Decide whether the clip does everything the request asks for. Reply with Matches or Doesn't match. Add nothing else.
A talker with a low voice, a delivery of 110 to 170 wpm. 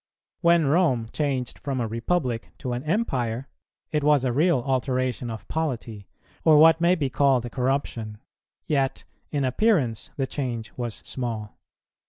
Matches